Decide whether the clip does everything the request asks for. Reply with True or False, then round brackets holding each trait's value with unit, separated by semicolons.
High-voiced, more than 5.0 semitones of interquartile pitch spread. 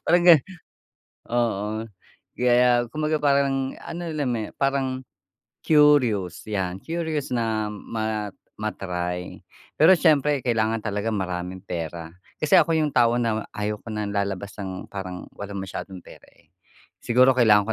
False (115 Hz; 5.4 semitones)